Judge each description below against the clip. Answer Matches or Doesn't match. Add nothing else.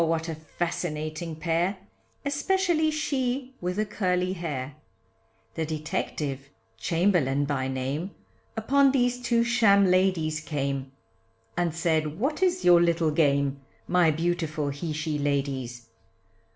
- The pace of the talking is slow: Matches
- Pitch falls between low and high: Matches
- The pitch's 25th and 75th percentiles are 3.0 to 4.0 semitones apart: Doesn't match